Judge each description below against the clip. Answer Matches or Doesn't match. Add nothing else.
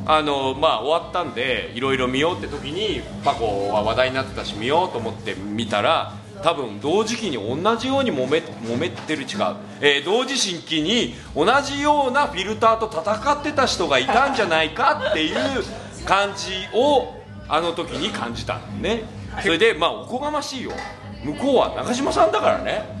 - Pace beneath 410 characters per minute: Matches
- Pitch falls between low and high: Matches